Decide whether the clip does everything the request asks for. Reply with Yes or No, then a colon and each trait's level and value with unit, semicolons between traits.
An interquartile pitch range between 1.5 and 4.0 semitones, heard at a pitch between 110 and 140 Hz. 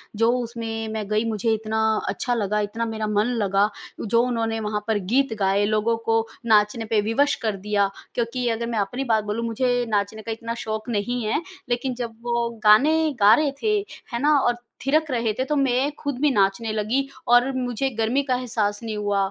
No: narrow, 2.5 semitones; high, 225 Hz